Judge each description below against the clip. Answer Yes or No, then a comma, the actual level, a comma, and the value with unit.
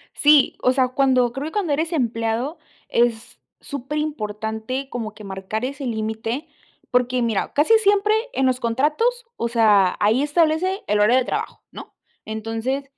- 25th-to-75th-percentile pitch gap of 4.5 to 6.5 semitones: Yes, average, 5.0 semitones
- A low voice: No, very high, 255 Hz